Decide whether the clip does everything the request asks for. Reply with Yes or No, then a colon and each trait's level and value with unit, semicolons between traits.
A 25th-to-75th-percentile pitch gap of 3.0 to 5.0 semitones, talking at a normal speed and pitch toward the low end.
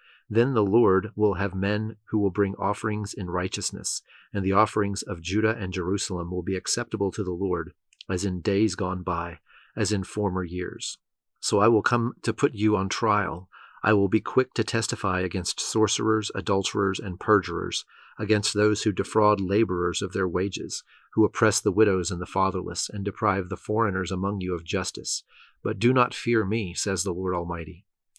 No: narrow, 2.5 semitones; average, 185 wpm; low, 100 Hz